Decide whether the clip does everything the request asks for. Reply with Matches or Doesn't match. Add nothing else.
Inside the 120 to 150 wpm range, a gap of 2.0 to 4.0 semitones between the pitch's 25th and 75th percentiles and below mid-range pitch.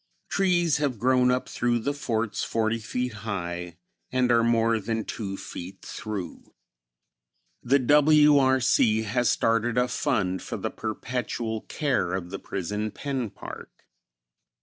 Matches